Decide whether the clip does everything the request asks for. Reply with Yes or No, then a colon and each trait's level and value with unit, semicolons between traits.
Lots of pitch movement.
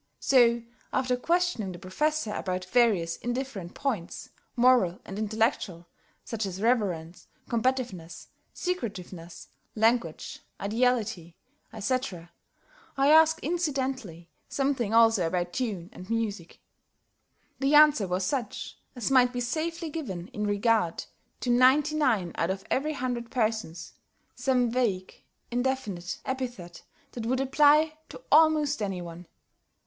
Yes: wide, 6.0 semitones